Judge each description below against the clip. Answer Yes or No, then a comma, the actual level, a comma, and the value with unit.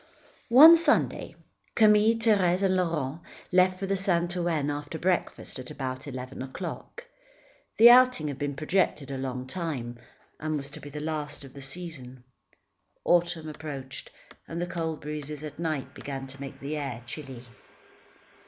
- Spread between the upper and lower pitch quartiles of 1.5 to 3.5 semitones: No, average, 4.6 semitones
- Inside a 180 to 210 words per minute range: No, average, 155 wpm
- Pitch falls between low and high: Yes, medium, 155 Hz